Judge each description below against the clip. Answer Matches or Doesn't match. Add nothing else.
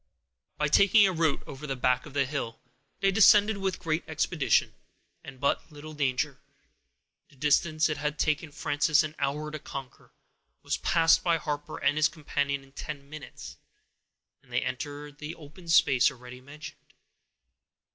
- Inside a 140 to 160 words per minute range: Matches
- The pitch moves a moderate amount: Doesn't match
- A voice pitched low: Doesn't match